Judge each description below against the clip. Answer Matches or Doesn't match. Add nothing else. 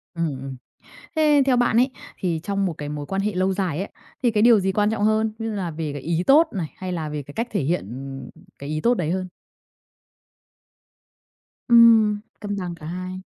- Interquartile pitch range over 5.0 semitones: Matches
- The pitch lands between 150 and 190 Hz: Matches